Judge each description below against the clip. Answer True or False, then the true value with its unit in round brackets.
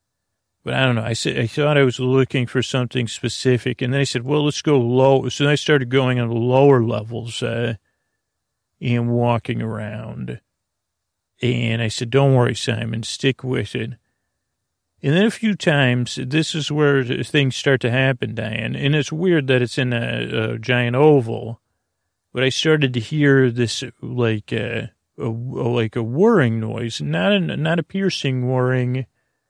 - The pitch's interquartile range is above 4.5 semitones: False (3.1 semitones)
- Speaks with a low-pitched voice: True (125 Hz)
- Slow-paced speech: False (175 wpm)